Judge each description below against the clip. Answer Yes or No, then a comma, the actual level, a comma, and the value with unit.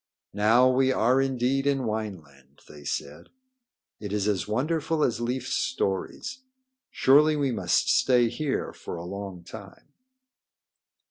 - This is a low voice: Yes, low, 120 Hz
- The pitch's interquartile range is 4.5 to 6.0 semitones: Yes, average, 5.2 semitones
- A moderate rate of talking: No, slow, 130 wpm